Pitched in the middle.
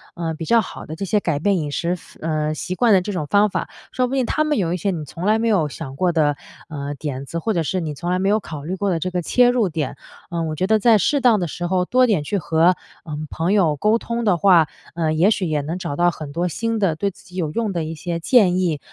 Yes: medium, 175 Hz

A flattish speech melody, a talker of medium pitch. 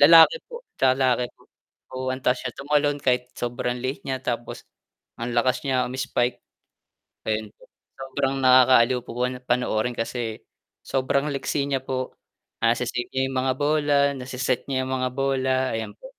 No: narrow, 1.6 semitones; low, 130 Hz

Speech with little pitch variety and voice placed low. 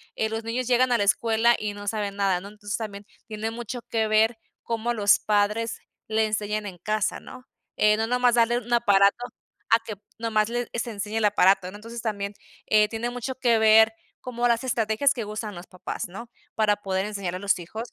No: narrow, 2.2 semitones; high, 220 Hz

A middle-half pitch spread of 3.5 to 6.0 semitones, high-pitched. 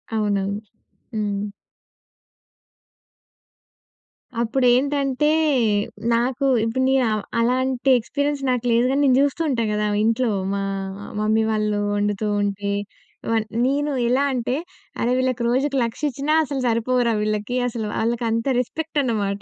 Yes: average, 3.8 semitones; high, 240 Hz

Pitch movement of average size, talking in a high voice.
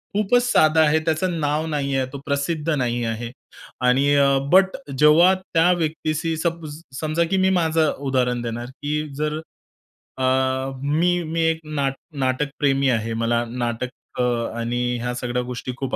No: average, 4.3 semitones; medium, 145 Hz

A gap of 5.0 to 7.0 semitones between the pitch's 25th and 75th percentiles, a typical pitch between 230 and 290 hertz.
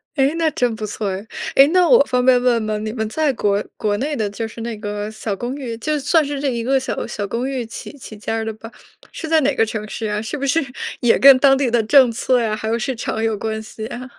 No: average, 3.7 semitones; high, 235 Hz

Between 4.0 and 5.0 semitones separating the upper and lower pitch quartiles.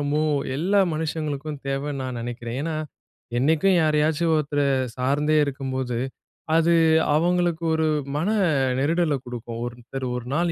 No: average, 3.5 semitones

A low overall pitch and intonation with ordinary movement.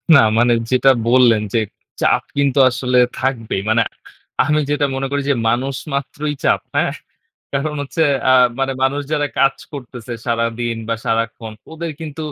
Yes: low, 130 Hz; average, 3.4 semitones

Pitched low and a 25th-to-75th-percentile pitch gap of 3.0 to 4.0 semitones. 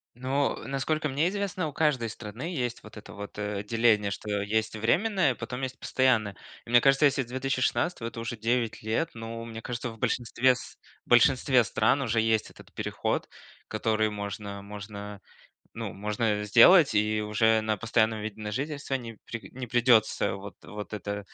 Yes: low, 115 Hz; average, 3.6 semitones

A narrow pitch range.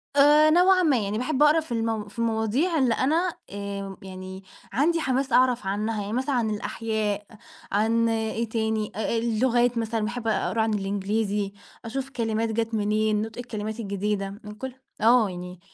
No: average, 3.1 semitones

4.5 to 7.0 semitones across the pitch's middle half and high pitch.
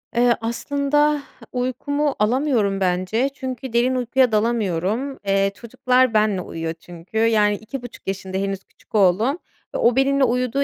Yes: average, 4.8 semitones; high, 235 Hz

